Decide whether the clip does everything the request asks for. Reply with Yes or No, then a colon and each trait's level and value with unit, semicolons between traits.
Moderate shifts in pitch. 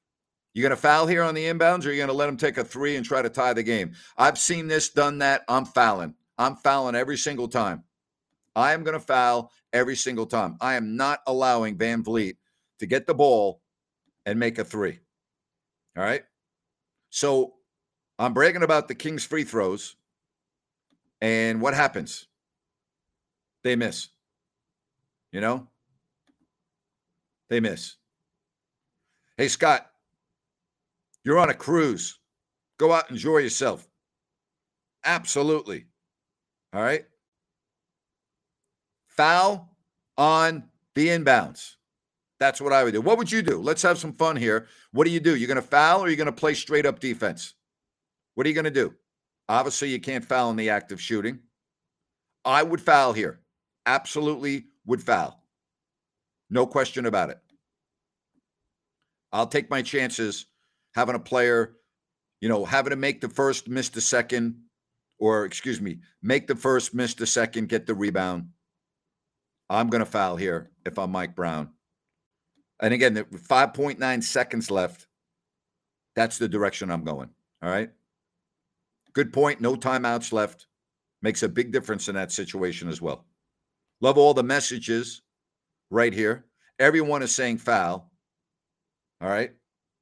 Yes: average, 4.5 semitones